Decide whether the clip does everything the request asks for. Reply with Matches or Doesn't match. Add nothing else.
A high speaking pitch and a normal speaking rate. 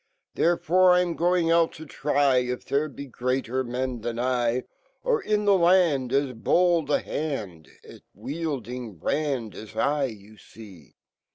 Doesn't match